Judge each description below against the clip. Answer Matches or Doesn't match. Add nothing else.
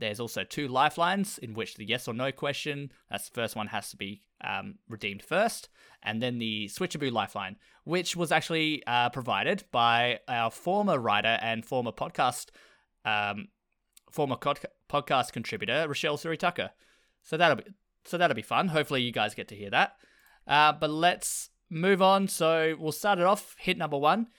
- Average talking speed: Matches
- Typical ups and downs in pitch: Doesn't match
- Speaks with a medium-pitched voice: Matches